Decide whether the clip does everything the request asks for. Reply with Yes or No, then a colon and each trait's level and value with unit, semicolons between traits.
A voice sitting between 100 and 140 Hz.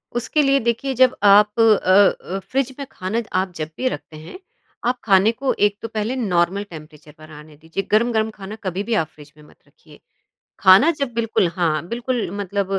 No: high, 205 Hz